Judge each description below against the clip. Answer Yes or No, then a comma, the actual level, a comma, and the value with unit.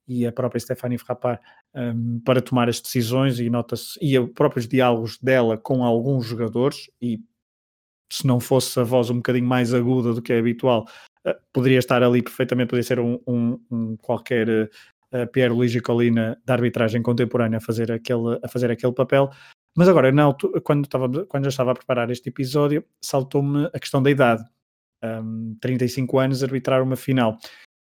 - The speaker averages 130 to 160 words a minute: No, average, 175 wpm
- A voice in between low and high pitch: No, low, 125 Hz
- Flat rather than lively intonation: Yes, narrow, 1.8 semitones